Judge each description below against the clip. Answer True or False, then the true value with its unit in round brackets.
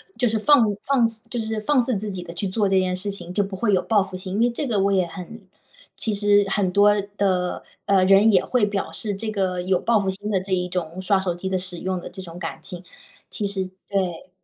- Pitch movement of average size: False (2.3 semitones)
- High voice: True (195 Hz)